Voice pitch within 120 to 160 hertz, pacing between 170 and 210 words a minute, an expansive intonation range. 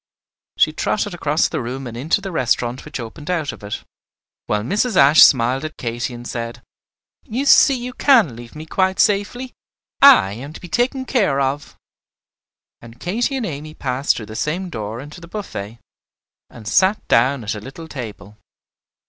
Yes: medium, 140 Hz; average, 175 wpm; wide, 8.2 semitones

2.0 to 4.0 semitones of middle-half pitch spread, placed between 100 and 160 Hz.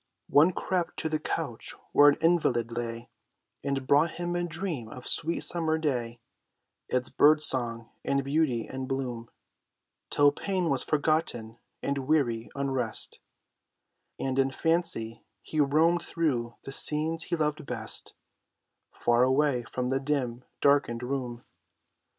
No: average, 4.4 semitones; medium, 140 Hz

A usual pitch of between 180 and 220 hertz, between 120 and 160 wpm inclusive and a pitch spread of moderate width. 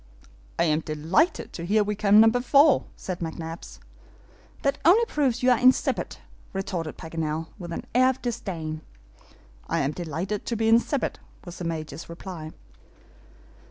No: high, 190 Hz; average, 150 wpm; wide, 6.9 semitones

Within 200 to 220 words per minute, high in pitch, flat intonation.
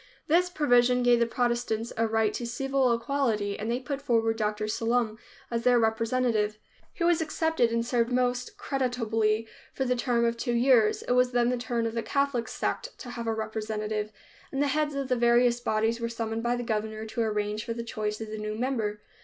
Yes: fast, 205 wpm; high, 235 Hz; narrow, 2.2 semitones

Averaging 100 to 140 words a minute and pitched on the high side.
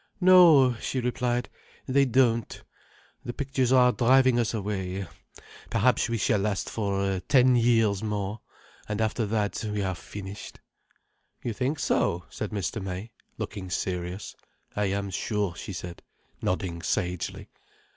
No: slow, 135 wpm; low, 105 Hz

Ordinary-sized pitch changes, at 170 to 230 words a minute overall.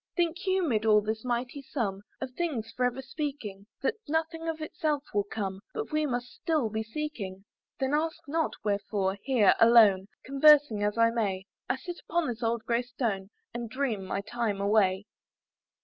No: wide, 6.1 semitones; average, 180 wpm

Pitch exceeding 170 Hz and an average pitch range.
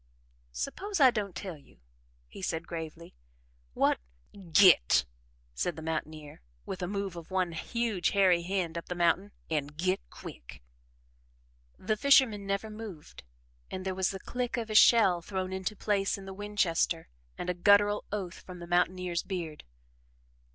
Yes: medium, 185 Hz; average, 3.2 semitones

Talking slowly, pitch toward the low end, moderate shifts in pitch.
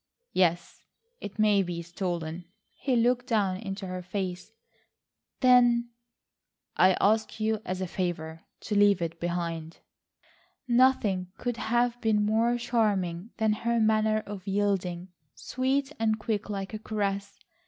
No: slow, 130 wpm; high, 205 Hz; average, 3.7 semitones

